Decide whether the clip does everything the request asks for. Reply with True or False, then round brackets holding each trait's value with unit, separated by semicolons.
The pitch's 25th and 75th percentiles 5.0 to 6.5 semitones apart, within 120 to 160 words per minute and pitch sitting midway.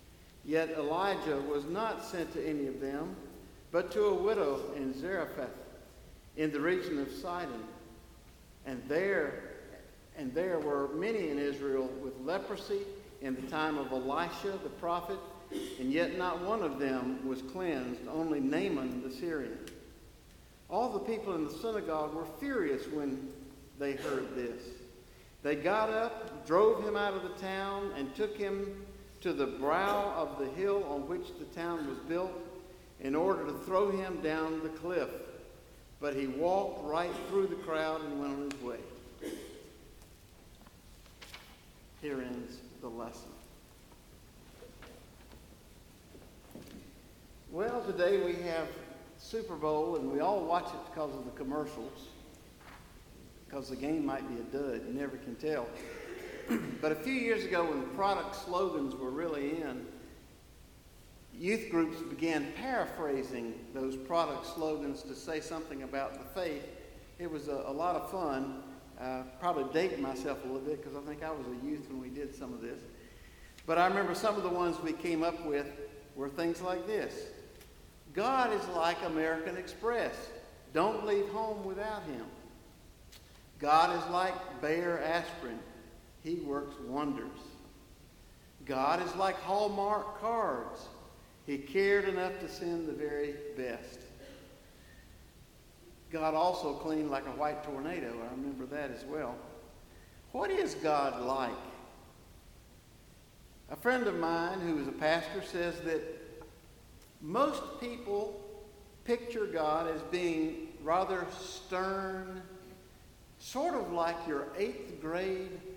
True (5.6 semitones; 140 wpm; 160 Hz)